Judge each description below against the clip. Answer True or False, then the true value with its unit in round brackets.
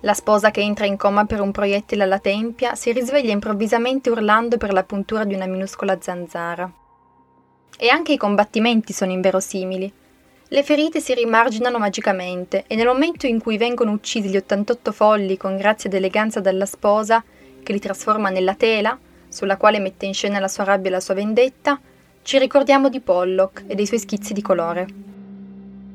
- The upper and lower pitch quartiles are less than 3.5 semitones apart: True (3.0 semitones)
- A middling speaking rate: False (175 wpm)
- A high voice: True (205 Hz)